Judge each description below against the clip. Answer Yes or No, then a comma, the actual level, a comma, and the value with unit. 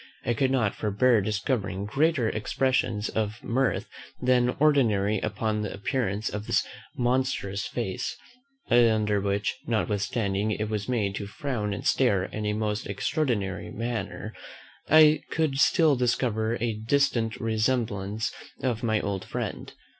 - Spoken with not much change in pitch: No, average, 3.4 semitones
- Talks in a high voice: No, low, 110 Hz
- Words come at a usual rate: No, slow, 130 wpm